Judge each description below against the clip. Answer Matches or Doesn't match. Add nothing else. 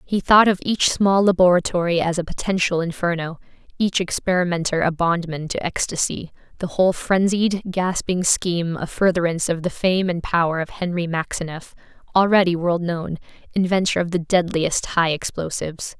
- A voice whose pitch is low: Doesn't match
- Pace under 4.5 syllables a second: Doesn't match